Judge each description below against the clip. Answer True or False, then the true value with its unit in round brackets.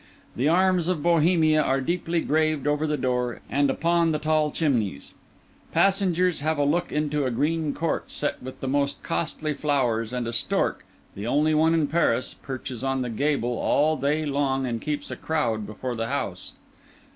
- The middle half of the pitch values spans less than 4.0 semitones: True (3.5 semitones)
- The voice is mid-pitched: True (145 Hz)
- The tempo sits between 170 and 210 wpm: True (180 wpm)